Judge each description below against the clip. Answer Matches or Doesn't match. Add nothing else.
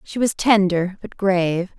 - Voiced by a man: Doesn't match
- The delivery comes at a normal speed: Matches